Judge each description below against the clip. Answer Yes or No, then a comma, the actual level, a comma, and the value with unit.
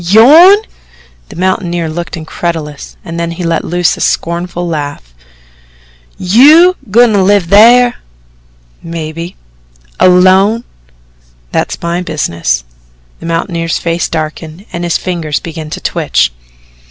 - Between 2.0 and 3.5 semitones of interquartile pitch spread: Yes, average, 3.0 semitones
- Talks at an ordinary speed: No, slow, 115 wpm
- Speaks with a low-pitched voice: No, medium, 170 Hz